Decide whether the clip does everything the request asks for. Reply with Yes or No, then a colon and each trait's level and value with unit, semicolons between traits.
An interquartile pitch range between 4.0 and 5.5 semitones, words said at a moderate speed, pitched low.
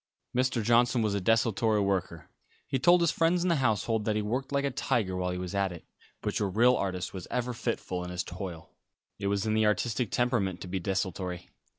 No: average, 4.6 semitones; fast, 220 wpm; low, 105 Hz